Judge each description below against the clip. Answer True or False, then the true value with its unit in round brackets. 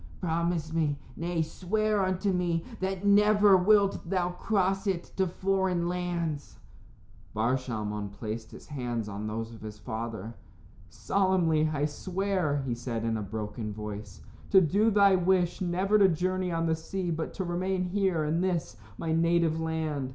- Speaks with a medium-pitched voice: True (170 Hz)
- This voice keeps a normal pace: True (160 wpm)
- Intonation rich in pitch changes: True (6.2 semitones)